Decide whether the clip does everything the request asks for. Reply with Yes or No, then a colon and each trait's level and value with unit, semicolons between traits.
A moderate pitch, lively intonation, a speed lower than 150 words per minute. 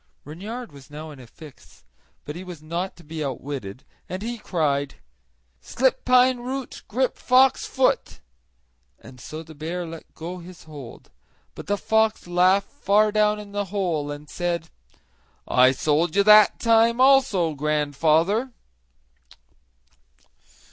Yes: medium, 175 Hz; wide, 6.0 semitones; average, 140 wpm